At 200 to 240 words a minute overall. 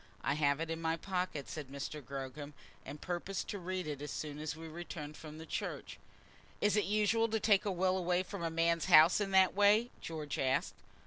Yes: fast, 205 wpm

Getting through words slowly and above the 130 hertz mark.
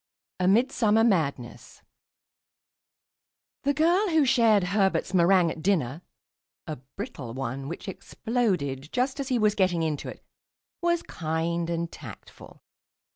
Yes: slow, 125 wpm; high, 190 Hz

